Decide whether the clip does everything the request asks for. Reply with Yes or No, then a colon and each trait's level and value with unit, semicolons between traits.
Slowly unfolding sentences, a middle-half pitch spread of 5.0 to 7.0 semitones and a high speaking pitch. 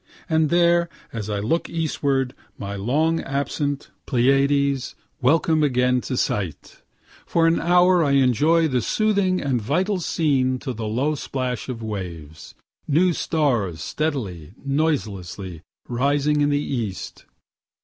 No: slow, 130 wpm; wide, 5.4 semitones; medium, 140 Hz